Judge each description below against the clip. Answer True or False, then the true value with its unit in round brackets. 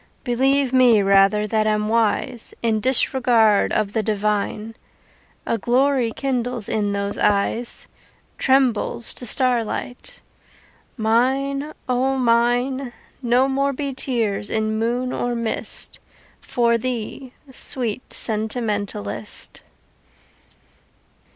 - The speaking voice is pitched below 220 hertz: False (235 Hz)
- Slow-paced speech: True (100 wpm)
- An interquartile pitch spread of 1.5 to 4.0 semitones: True (3.1 semitones)